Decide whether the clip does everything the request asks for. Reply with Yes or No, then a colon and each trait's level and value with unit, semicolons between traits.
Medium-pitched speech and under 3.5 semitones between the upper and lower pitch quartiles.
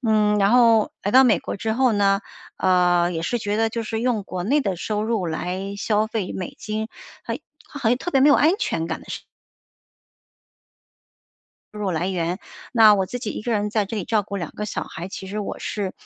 No: high, 210 Hz; average, 2.9 semitones